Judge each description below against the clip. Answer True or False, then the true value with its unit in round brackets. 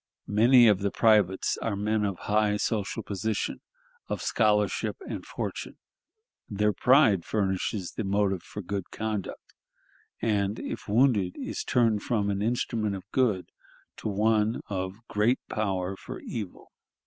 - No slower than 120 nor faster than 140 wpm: True (135 wpm)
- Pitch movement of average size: False (2.0 semitones)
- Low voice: True (105 Hz)